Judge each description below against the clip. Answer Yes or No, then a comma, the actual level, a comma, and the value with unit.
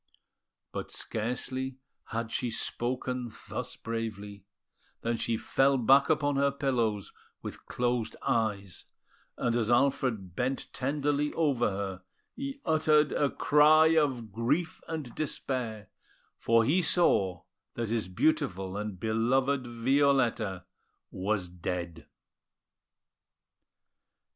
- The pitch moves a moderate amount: Yes, average, 4.6 semitones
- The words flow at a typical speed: No, slow, 105 wpm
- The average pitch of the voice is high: No, low, 120 Hz